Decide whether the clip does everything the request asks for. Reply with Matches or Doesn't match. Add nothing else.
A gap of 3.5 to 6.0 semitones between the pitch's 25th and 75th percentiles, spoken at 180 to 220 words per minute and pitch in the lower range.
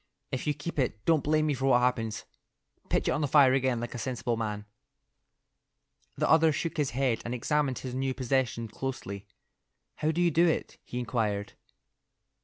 Matches